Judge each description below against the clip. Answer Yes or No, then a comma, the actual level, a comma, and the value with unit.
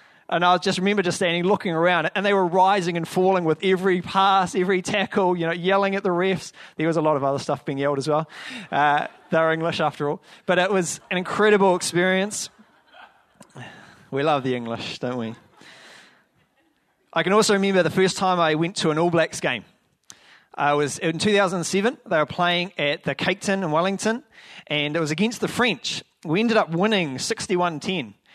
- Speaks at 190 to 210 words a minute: Yes, average, 195 wpm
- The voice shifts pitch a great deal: No, average, 3.7 semitones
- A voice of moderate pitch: Yes, medium, 180 Hz